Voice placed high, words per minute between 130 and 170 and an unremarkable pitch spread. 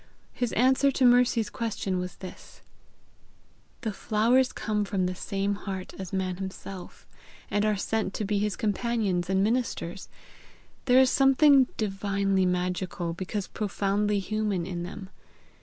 Yes: high, 200 Hz; average, 140 wpm; average, 3.1 semitones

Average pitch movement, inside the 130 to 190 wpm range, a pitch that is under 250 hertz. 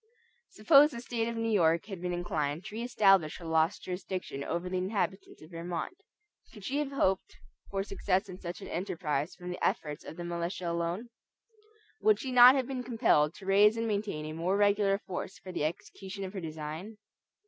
No: average, 4.1 semitones; average, 200 wpm; high, 190 Hz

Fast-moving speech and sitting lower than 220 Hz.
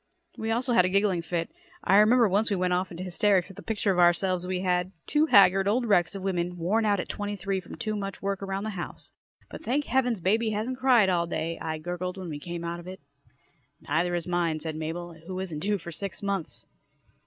Yes: fast, 230 wpm; high, 190 Hz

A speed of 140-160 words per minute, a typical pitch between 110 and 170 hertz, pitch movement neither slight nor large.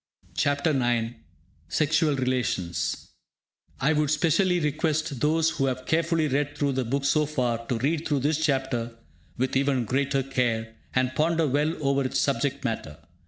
Yes: average, 155 wpm; medium, 140 Hz; average, 3.2 semitones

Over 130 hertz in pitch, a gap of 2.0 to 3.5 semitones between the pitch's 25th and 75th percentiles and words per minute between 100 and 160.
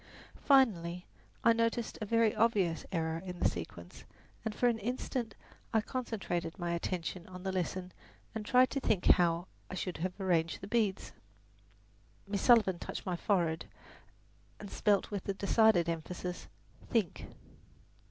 No: high, 190 Hz; average, 4.3 semitones; average, 140 wpm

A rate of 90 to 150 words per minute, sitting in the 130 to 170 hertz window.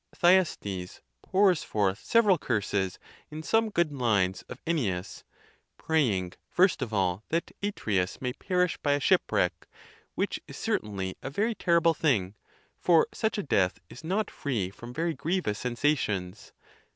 Yes: average, 140 wpm; low, 135 Hz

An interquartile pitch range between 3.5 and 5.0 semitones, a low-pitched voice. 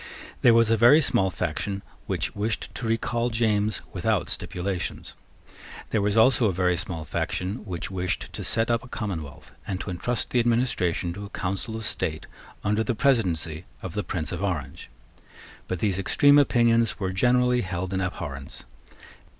Yes: average, 4.3 semitones; low, 100 Hz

